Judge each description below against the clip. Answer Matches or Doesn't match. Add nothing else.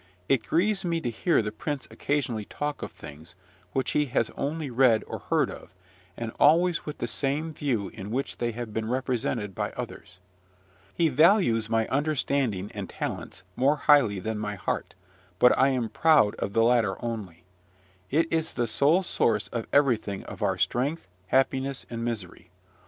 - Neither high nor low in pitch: Doesn't match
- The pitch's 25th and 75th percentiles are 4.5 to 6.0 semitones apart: Matches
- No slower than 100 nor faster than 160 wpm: Doesn't match